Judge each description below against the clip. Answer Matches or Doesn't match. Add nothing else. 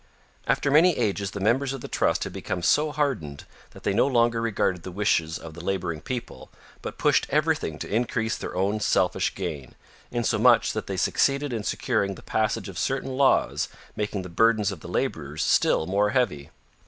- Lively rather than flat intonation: Matches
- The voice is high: Doesn't match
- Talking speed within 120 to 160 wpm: Doesn't match